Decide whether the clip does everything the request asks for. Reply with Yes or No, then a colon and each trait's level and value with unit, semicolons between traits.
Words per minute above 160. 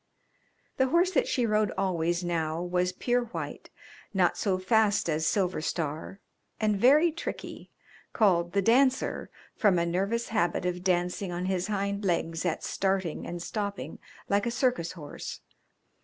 No: average, 150 wpm